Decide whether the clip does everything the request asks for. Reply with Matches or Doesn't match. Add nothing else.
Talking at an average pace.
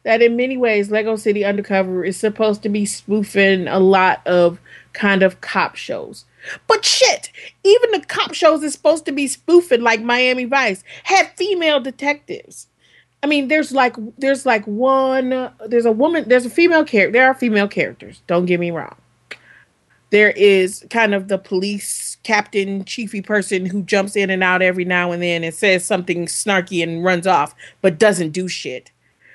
Matches